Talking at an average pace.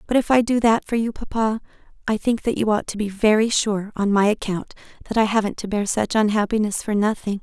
No: fast, 235 wpm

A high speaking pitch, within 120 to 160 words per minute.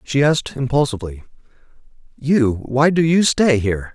No: low, 130 Hz; slow, 135 wpm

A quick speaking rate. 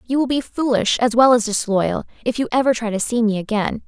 Yes: fast, 250 wpm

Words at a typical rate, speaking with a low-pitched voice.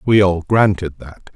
Yes: average, 180 wpm; very low, 95 Hz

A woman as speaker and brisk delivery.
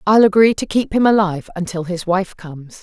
Yes: female; fast, 215 wpm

